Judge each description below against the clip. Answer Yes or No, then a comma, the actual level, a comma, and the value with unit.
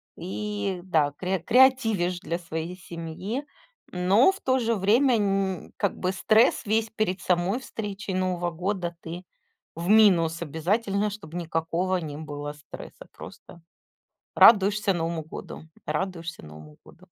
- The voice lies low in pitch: No, medium, 185 Hz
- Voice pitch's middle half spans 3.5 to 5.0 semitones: Yes, average, 3.9 semitones